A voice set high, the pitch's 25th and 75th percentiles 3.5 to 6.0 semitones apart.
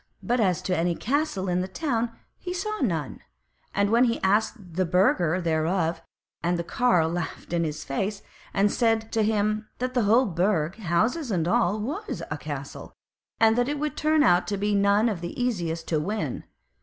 Yes: high, 200 Hz; average, 5.2 semitones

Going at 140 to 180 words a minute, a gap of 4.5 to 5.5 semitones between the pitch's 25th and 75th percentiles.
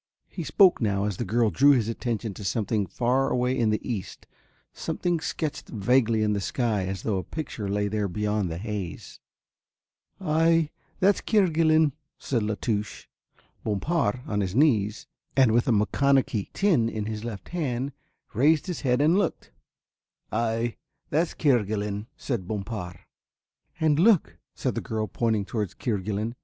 Yes: average, 155 wpm; average, 5.1 semitones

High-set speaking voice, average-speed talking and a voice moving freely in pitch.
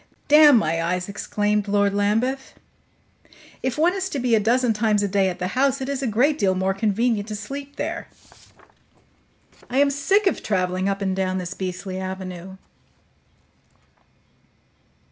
Yes: high, 210 Hz; average, 160 wpm; wide, 5.9 semitones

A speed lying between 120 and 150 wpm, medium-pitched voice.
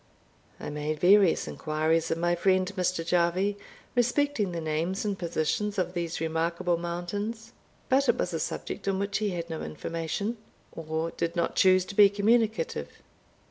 No: average, 160 wpm; medium, 180 Hz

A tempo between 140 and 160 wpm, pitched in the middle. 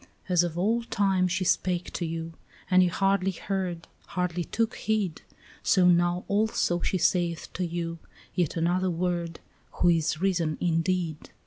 Yes: average, 150 wpm; medium, 180 Hz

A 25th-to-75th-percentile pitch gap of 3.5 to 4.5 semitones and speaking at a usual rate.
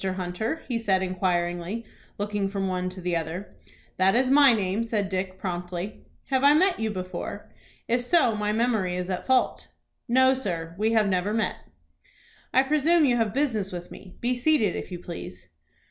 No: average, 4.9 semitones; average, 175 wpm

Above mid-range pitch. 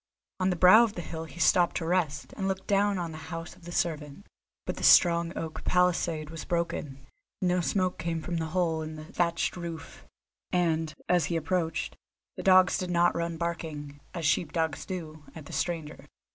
No: medium, 170 Hz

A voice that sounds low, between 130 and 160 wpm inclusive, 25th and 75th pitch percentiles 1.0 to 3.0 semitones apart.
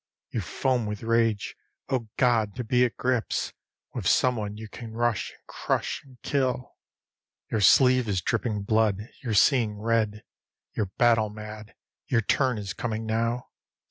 Yes: low, 115 Hz; average, 150 wpm; narrow, 2.6 semitones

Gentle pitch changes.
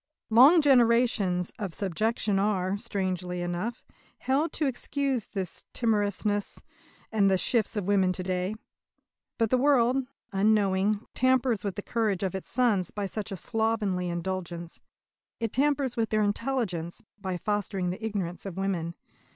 No: average, 3.8 semitones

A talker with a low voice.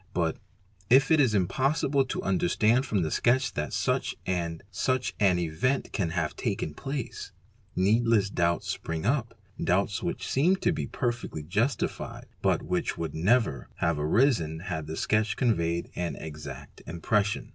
Yes: very low, 95 Hz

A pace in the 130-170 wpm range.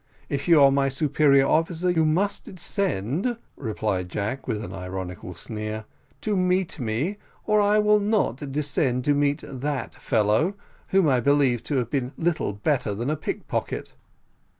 Yes: average, 155 wpm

